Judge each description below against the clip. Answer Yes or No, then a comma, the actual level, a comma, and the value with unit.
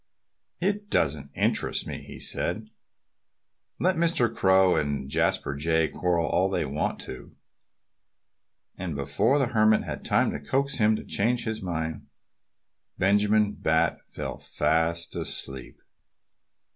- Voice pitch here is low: Yes, very low, 95 Hz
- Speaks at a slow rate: Yes, slow, 125 wpm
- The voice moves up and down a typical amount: No, wide, 6.1 semitones